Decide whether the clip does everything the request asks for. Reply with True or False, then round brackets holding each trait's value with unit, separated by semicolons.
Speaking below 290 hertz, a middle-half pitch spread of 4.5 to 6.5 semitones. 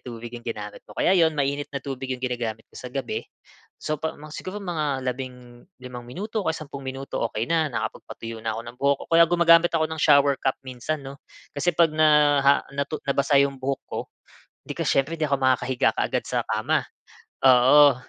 False (140 Hz; 3.6 semitones)